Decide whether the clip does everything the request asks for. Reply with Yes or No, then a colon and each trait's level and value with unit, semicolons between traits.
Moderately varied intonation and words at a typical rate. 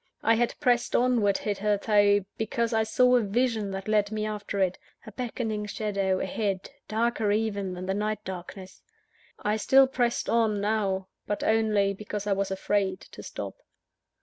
No: narrow, 2.0 semitones; average, 160 wpm